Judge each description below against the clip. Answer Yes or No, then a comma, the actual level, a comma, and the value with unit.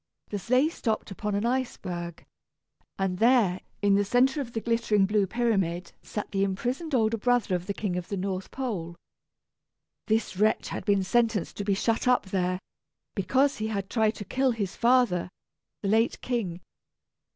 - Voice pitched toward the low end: No, high, 210 Hz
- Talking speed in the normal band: Yes, average, 170 wpm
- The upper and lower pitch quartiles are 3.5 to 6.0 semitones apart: Yes, average, 3.8 semitones